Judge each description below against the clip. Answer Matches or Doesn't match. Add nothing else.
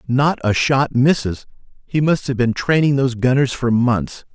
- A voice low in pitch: Matches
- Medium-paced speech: Matches